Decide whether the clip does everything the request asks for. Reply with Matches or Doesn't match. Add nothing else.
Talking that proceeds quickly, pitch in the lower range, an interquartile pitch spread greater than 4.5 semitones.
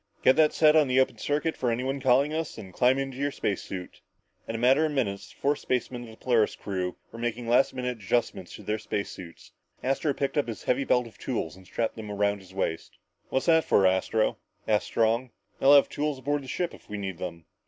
Matches